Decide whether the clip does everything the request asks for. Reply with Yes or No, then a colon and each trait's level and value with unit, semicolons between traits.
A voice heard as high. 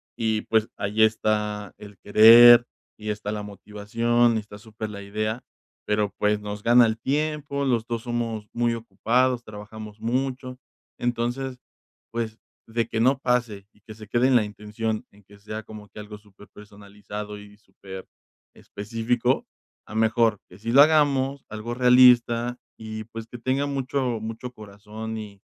No: low, 110 Hz